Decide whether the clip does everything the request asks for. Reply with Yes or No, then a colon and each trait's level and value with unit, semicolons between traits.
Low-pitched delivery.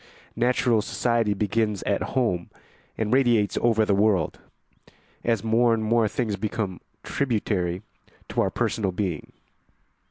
Yes: low, 110 Hz